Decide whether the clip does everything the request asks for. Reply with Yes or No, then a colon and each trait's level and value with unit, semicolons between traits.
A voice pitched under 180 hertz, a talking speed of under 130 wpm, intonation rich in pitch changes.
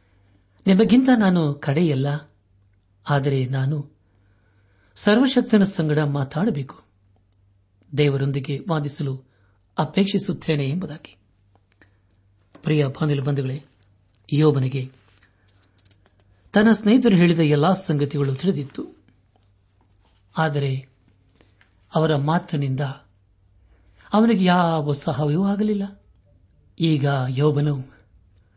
Yes: low, 135 Hz; slow, 65 wpm; wide, 7.9 semitones